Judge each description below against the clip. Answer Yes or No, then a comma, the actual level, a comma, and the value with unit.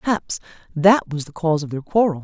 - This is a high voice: No, medium, 170 Hz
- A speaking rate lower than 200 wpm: No, fast, 215 wpm